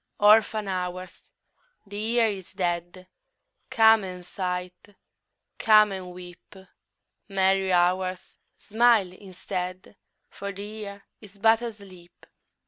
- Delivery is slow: Yes, slow, 105 wpm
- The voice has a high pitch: Yes, high, 195 Hz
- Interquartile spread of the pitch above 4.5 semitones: No, narrow, 2.6 semitones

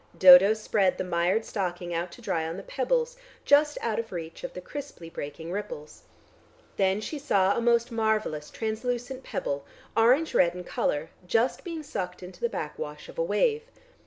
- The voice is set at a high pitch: Yes, high, 215 Hz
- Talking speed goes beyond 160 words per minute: Yes, average, 175 wpm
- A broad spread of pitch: Yes, wide, 6.8 semitones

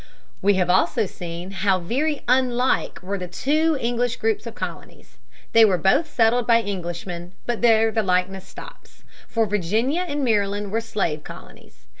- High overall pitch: Yes, high, 215 Hz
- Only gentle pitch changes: No, average, 4.7 semitones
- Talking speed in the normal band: Yes, average, 160 wpm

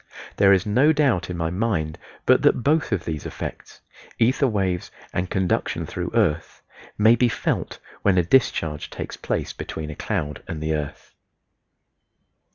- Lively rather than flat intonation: Yes, wide, 6.0 semitones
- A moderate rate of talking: Yes, average, 160 wpm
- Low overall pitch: Yes, very low, 95 Hz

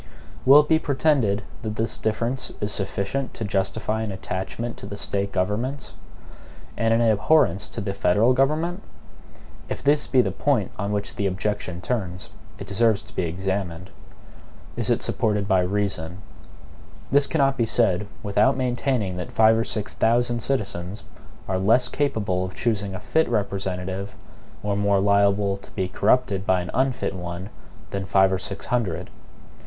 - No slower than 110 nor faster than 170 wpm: Yes, average, 160 wpm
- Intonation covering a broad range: No, average, 3.8 semitones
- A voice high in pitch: No, low, 105 Hz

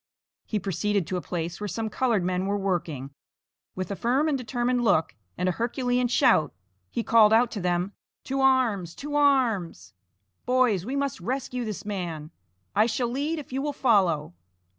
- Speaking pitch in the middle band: No, high, 220 Hz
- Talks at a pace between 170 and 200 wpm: Yes, average, 175 wpm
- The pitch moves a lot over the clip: Yes, wide, 5.8 semitones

